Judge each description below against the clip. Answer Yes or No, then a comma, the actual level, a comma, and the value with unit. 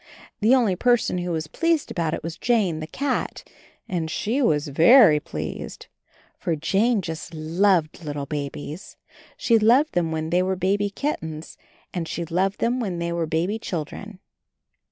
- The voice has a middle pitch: Yes, medium, 175 Hz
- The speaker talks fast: No, average, 160 wpm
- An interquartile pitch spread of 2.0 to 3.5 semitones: No, average, 5.2 semitones